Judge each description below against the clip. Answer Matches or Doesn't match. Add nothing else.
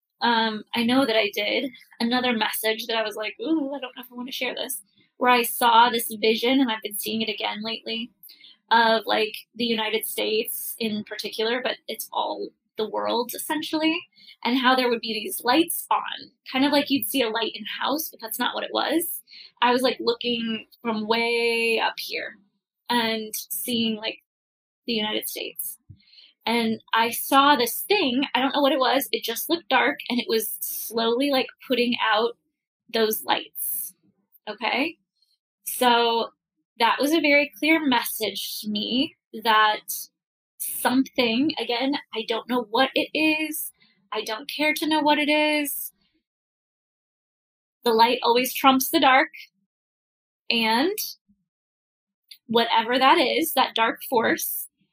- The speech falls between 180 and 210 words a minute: Doesn't match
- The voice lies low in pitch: Doesn't match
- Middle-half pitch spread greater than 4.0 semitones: Doesn't match